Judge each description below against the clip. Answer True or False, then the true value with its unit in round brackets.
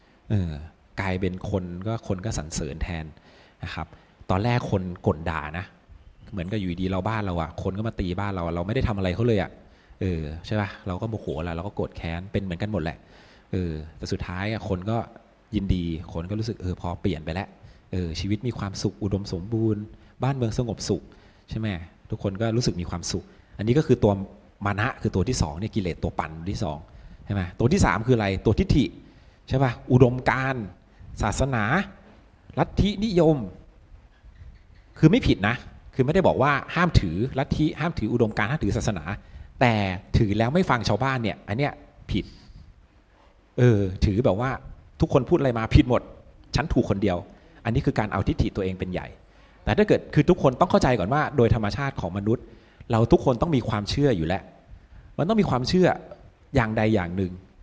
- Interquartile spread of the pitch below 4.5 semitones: True (4.1 semitones)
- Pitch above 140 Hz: False (100 Hz)